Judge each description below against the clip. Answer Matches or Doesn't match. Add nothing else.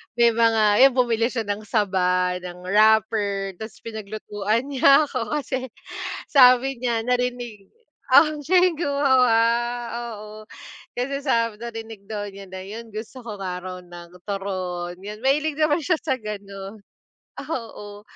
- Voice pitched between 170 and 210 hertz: Doesn't match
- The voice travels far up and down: Doesn't match